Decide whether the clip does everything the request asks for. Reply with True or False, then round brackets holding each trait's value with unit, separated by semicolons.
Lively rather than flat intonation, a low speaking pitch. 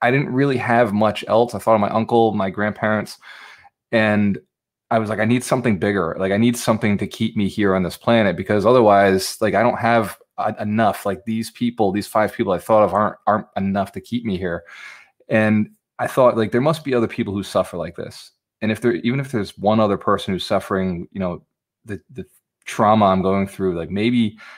False (2.8 semitones; 110 Hz)